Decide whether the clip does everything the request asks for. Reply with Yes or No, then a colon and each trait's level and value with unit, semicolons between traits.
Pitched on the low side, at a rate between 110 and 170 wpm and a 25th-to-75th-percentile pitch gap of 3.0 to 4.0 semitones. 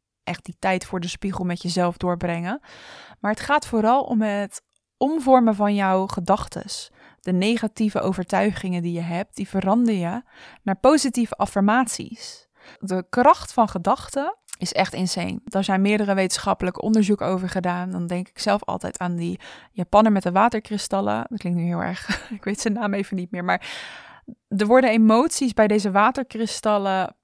No: high, 200 Hz; average, 165 wpm; average, 3.4 semitones